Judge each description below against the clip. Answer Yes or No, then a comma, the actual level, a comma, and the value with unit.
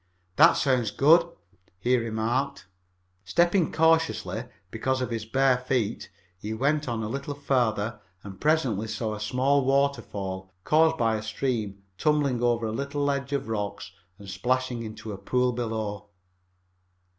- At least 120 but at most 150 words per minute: Yes, average, 145 wpm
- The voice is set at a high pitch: No, low, 120 Hz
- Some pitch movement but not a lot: Yes, average, 4.3 semitones